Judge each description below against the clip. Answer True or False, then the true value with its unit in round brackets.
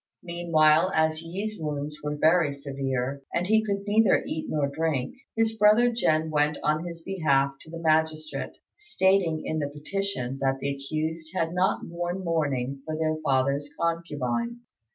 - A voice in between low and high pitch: True (160 Hz)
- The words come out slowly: False (155 wpm)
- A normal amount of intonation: True (3.6 semitones)